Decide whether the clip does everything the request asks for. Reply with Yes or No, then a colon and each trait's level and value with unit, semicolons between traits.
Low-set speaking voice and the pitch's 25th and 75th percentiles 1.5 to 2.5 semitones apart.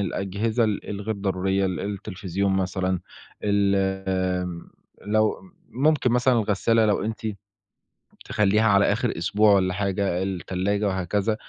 Yes: low, 100 Hz; narrow, 2.1 semitones